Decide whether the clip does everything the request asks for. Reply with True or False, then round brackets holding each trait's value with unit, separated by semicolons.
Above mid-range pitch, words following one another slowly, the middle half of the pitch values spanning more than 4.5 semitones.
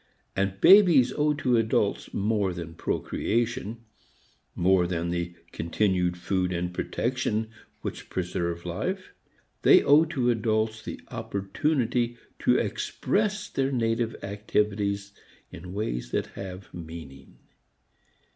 False (105 Hz; 110 wpm; 5.0 semitones)